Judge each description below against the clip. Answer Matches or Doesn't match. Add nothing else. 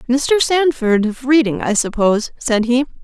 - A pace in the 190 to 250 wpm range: Doesn't match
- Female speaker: Matches